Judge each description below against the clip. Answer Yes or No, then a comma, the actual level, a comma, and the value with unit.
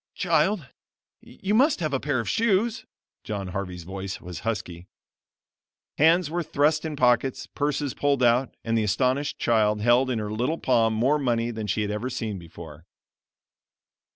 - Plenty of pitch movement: Yes, wide, 6.0 semitones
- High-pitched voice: No, low, 120 Hz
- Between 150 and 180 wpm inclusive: Yes, average, 160 wpm